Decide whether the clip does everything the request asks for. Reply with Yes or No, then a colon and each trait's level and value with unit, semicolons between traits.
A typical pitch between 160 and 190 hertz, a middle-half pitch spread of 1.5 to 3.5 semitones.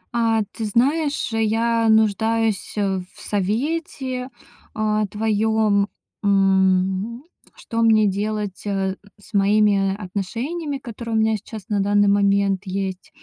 No: high, 215 Hz; narrow, 2.4 semitones